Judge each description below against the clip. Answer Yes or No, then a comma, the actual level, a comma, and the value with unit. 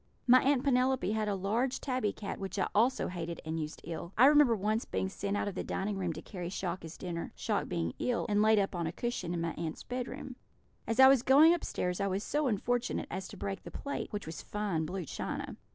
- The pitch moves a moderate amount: No, wide, 5.8 semitones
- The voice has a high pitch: Yes, high, 205 Hz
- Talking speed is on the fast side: Yes, fast, 230 wpm